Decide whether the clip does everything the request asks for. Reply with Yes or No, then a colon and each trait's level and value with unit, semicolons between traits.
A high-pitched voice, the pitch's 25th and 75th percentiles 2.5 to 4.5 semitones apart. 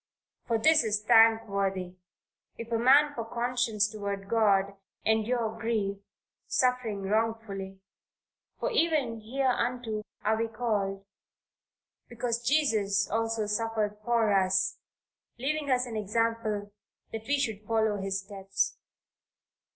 Yes: high, 225 Hz; average, 2.8 semitones